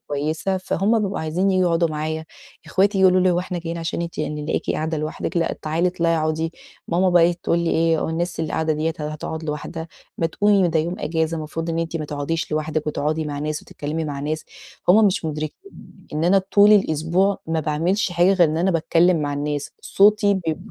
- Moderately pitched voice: Yes, medium, 165 Hz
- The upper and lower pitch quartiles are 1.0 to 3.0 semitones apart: Yes, average, 2.7 semitones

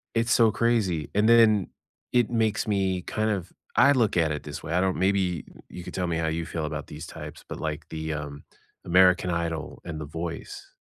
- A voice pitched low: Yes, very low, 90 Hz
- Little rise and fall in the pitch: No, average, 4.8 semitones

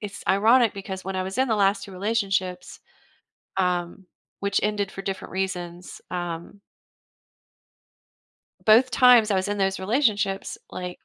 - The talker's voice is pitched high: Yes, high, 195 Hz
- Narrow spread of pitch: Yes, narrow, 2.2 semitones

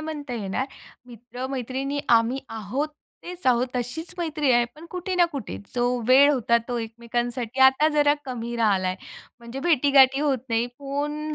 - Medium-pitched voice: No, very high, 260 Hz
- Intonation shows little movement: No, average, 3.6 semitones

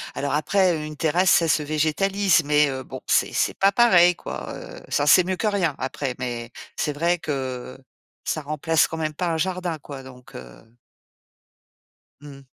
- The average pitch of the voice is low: No, medium, 155 Hz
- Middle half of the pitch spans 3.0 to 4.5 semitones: Yes, average, 4.2 semitones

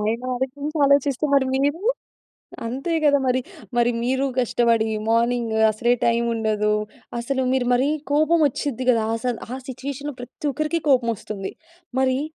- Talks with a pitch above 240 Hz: Yes, very high, 255 Hz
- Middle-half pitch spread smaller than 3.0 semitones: No, average, 3.3 semitones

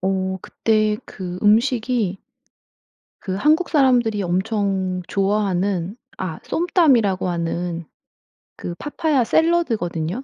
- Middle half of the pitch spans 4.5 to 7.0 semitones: Yes, average, 5.1 semitones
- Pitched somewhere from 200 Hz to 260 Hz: Yes, high, 205 Hz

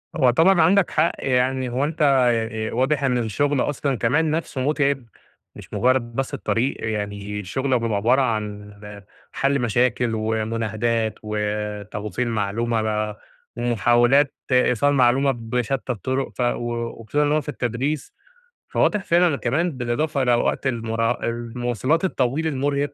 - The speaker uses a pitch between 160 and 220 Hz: No, low, 125 Hz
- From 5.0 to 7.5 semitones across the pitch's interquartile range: No, average, 3.7 semitones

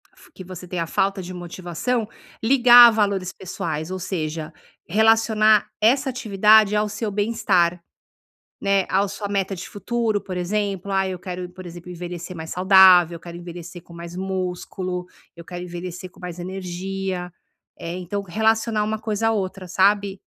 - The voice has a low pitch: No, high, 190 Hz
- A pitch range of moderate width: Yes, average, 3.0 semitones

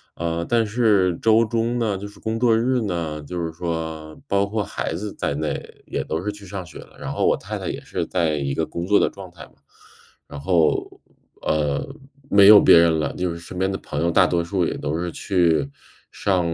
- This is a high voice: No, very low, 90 Hz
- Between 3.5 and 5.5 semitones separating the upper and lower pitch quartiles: Yes, average, 4.0 semitones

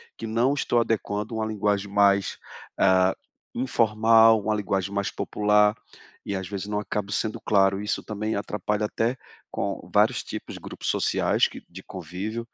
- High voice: No, low, 105 Hz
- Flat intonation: Yes, narrow, 1.9 semitones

